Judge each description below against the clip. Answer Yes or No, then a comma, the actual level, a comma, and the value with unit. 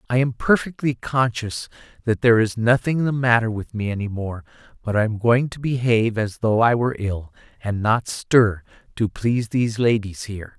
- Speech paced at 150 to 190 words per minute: Yes, average, 185 wpm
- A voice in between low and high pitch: No, low, 115 Hz